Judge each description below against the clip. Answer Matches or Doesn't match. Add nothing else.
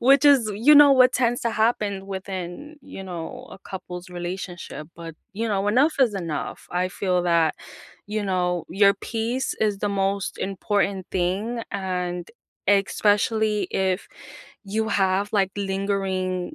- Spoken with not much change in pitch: Doesn't match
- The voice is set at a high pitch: Matches